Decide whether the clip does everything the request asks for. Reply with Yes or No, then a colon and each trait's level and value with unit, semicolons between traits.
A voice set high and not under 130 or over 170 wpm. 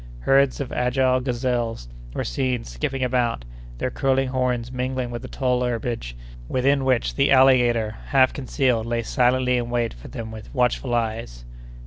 No: low, 125 Hz; average, 155 wpm